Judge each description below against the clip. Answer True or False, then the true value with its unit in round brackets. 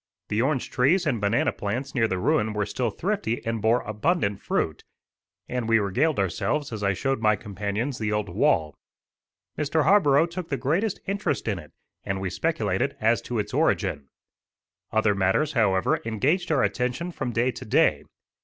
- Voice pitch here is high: False (115 Hz)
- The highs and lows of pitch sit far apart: True (6.0 semitones)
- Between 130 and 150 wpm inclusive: False (170 wpm)